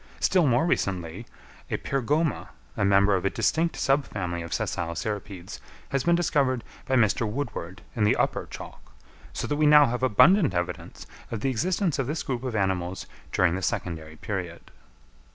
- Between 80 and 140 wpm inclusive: No, average, 170 wpm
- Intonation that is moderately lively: No, wide, 7.3 semitones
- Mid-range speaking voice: No, low, 115 Hz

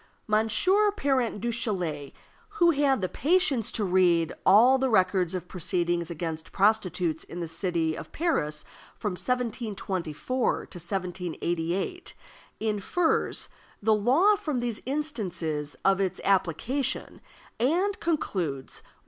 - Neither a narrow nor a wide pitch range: No, wide, 7.1 semitones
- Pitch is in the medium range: No, high, 200 Hz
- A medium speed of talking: No, slow, 115 wpm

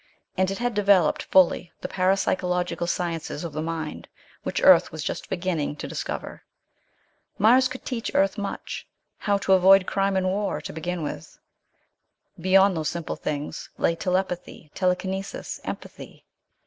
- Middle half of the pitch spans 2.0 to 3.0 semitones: Yes, narrow, 2.6 semitones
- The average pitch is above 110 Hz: Yes, medium, 185 Hz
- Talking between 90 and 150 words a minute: Yes, average, 145 wpm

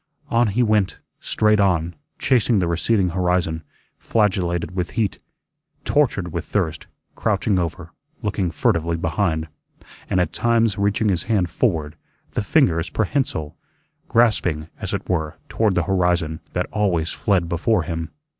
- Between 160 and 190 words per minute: No, slow, 135 wpm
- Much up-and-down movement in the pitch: No, average, 4.3 semitones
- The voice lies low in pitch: Yes, very low, 90 Hz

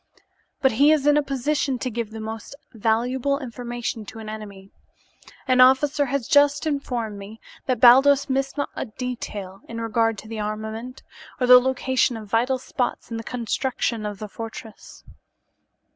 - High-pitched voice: Yes, high, 240 Hz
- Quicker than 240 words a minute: No, average, 170 wpm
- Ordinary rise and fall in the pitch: Yes, average, 3.3 semitones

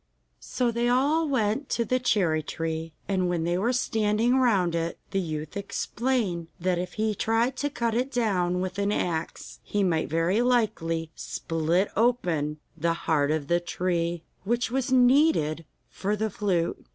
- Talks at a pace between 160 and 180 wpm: Yes, average, 165 wpm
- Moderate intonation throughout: No, wide, 6.2 semitones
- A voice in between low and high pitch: No, high, 195 Hz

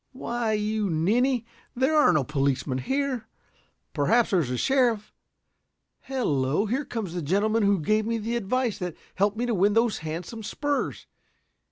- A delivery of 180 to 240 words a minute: No, average, 160 wpm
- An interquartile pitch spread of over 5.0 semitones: Yes, wide, 5.5 semitones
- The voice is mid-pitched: No, high, 215 Hz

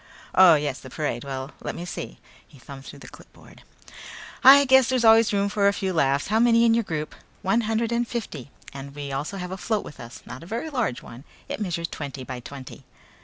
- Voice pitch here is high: No, medium, 175 Hz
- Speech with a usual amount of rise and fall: No, wide, 8.4 semitones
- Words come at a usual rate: No, fast, 220 wpm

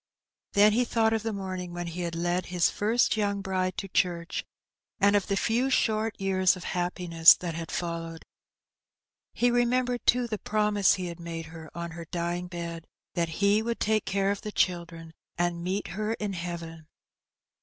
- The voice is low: No, medium, 185 Hz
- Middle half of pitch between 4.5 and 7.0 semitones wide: No, average, 3.6 semitones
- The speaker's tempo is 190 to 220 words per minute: Yes, average, 195 wpm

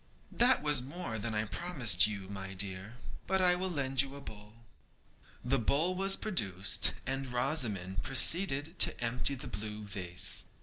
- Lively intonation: Yes, wide, 6.8 semitones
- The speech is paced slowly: No, average, 160 wpm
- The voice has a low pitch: Yes, low, 125 Hz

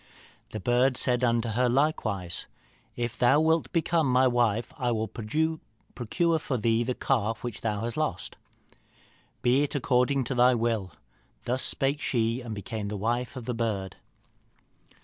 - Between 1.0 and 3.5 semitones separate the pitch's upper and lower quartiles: Yes, average, 2.8 semitones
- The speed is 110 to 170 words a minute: Yes, average, 155 wpm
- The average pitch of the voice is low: Yes, low, 120 Hz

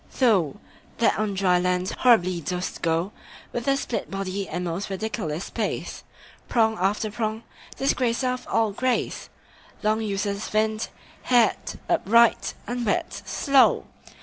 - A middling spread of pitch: Yes, average, 3.9 semitones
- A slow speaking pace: Yes, slow, 125 wpm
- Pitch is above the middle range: Yes, high, 215 Hz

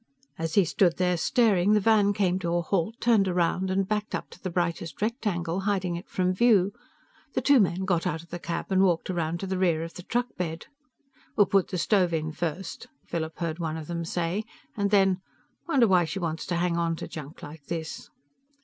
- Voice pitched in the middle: Yes, medium, 180 Hz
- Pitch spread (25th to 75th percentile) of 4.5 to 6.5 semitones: No, average, 2.7 semitones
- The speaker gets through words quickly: Yes, fast, 210 wpm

